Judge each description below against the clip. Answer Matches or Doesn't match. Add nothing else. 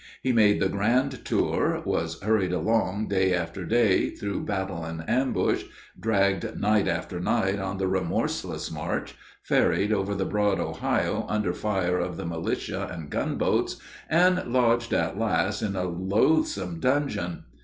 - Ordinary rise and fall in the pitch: Matches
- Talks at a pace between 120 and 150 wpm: Matches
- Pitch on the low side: Matches